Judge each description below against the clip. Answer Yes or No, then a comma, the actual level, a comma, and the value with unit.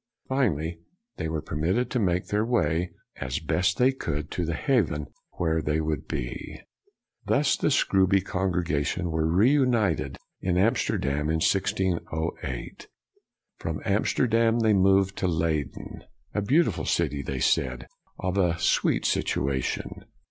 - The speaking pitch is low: Yes, very low, 90 Hz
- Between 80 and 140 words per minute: Yes, slow, 135 wpm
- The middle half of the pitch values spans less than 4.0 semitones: No, average, 4.3 semitones